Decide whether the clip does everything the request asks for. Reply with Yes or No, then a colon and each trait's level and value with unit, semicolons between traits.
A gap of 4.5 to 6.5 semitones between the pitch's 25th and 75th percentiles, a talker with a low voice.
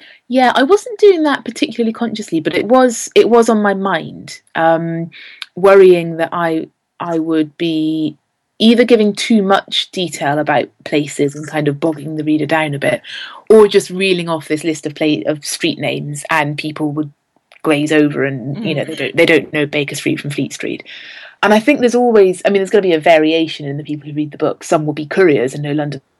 No: average, 5.0 semitones; medium, 160 Hz